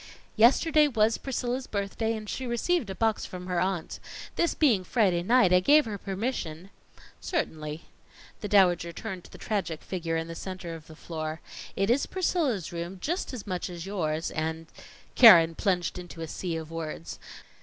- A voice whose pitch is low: No, high, 190 Hz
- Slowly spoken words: No, average, 175 wpm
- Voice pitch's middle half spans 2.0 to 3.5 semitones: No, wide, 5.4 semitones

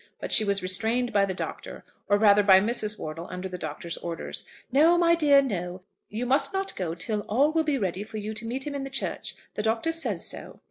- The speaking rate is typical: No, fast, 230 wpm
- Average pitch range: No, wide, 6.4 semitones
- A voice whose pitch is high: Yes, high, 215 Hz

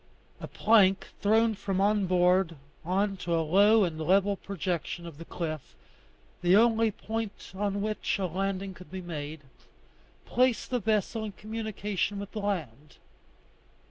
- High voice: Yes, high, 195 Hz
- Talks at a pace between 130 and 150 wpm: Yes, average, 145 wpm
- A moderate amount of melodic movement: Yes, average, 3.2 semitones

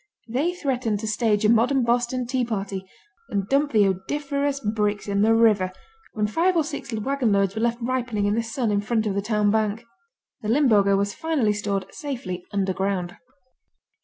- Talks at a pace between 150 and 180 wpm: Yes, average, 175 wpm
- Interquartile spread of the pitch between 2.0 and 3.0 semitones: No, average, 3.9 semitones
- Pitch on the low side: No, high, 220 Hz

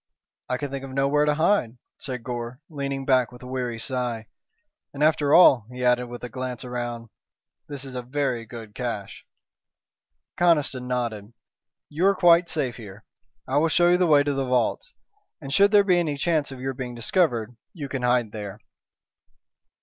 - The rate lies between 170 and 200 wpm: Yes, average, 180 wpm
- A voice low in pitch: Yes, low, 130 Hz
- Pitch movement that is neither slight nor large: Yes, average, 3.4 semitones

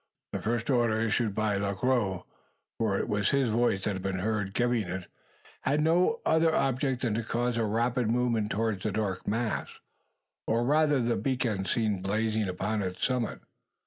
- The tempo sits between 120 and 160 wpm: No, average, 175 wpm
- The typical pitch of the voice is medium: No, low, 115 Hz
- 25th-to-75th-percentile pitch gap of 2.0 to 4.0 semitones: Yes, average, 3.2 semitones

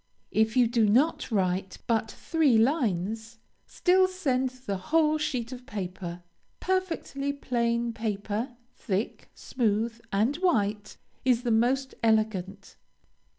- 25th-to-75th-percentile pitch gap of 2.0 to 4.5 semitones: Yes, average, 4.1 semitones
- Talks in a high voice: Yes, high, 235 Hz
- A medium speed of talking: No, slow, 115 wpm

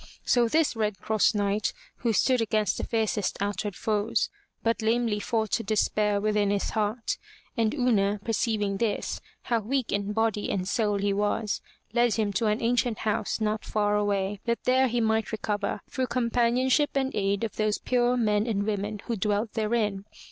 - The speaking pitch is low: No, high, 215 Hz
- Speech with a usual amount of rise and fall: No, narrow, 2.2 semitones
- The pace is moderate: Yes, average, 170 wpm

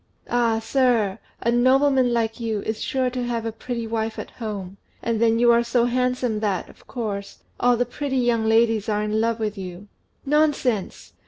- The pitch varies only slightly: Yes, narrow, 2.0 semitones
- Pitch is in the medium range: No, high, 230 Hz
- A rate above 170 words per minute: Yes, average, 185 wpm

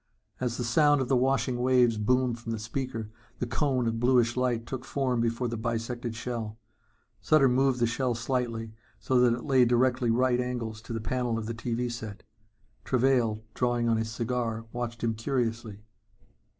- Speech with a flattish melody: Yes, narrow, 1.8 semitones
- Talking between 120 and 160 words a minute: No, average, 180 wpm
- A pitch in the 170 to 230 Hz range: No, low, 120 Hz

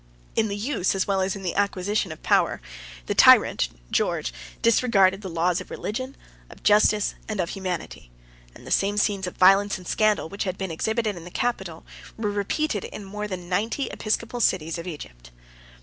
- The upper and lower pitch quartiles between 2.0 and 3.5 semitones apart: Yes, average, 2.7 semitones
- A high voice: Yes, high, 195 Hz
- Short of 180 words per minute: No, average, 185 wpm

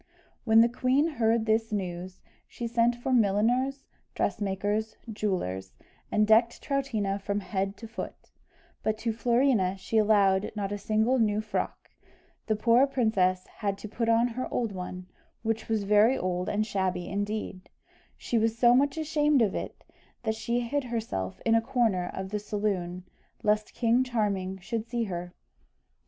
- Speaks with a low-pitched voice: No, high, 220 Hz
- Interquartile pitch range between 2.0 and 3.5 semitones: Yes, average, 3.2 semitones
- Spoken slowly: No, average, 160 wpm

